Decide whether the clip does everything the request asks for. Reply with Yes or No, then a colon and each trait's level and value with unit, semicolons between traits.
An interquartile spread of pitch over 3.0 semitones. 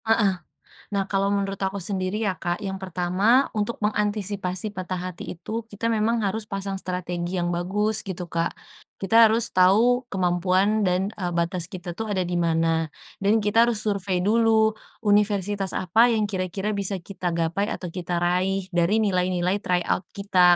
No: average, 2.7 semitones